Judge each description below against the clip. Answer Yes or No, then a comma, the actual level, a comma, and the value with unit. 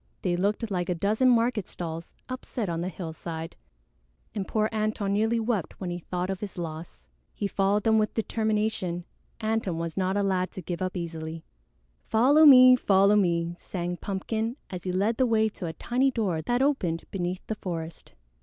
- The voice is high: Yes, high, 195 Hz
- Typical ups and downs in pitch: Yes, average, 4.0 semitones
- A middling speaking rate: Yes, average, 180 wpm